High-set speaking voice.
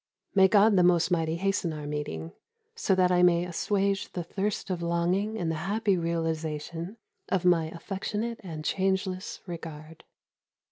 No: medium, 175 Hz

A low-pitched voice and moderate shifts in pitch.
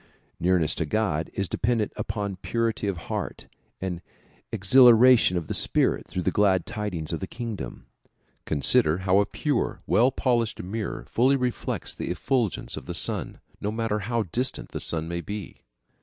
Yes: low, 105 Hz; average, 4.6 semitones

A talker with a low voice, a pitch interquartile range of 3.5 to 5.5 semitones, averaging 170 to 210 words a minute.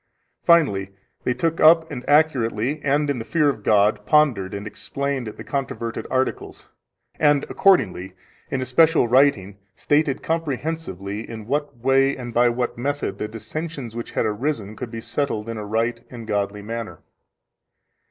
No: low, 125 Hz; average, 5.1 semitones; average, 155 wpm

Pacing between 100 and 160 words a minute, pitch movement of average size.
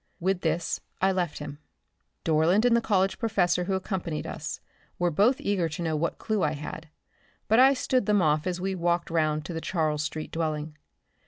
No: average, 190 wpm; average, 3.7 semitones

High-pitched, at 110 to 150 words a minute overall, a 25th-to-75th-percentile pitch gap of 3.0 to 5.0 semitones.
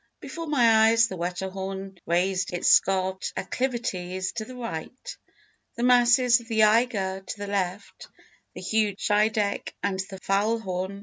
Yes: high, 200 Hz; average, 140 wpm; average, 3.4 semitones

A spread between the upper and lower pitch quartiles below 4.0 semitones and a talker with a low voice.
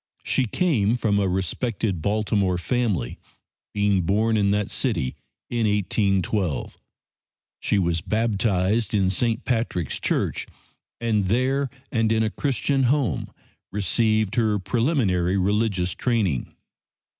Yes: average, 3.5 semitones; low, 105 Hz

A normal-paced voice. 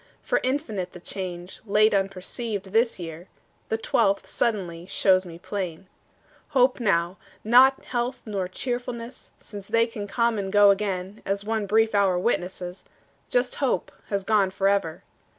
Yes: average, 150 wpm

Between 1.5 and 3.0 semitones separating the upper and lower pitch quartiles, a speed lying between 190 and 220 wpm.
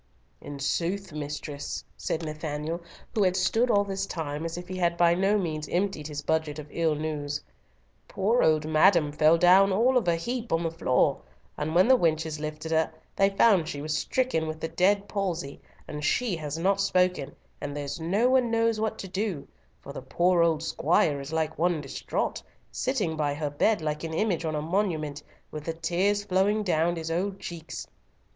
No: average, 4.2 semitones; average, 195 wpm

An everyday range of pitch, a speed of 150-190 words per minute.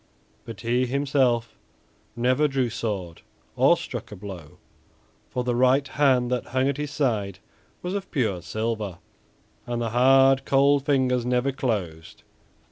No: average, 3.3 semitones; average, 140 wpm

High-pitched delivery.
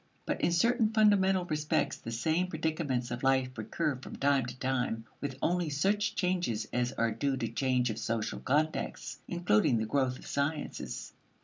No: medium, 140 Hz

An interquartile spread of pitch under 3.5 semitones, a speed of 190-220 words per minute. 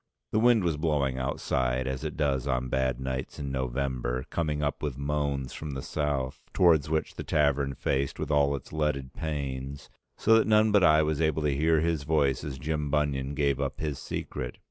Yes: average, 2.7 semitones; average, 195 wpm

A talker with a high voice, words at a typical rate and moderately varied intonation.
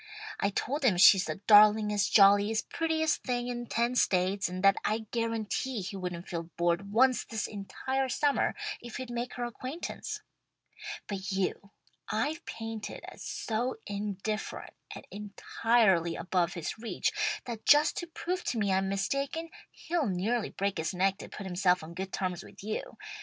Yes: high, 215 Hz; average, 160 wpm; average, 4.2 semitones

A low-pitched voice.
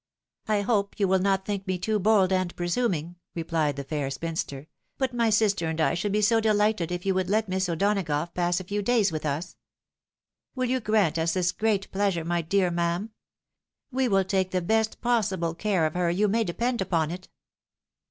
No: high, 190 Hz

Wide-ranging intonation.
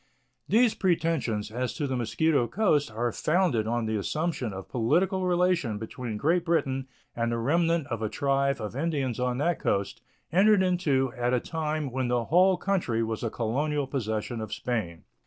Yes: wide, 6.2 semitones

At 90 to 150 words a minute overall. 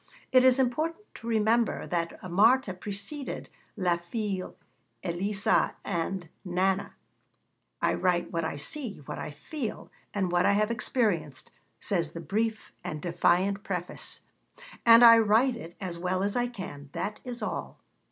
Yes: average, 145 wpm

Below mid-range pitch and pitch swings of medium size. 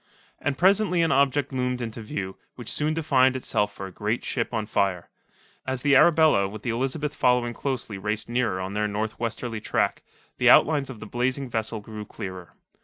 Yes: low, 120 Hz; average, 4.3 semitones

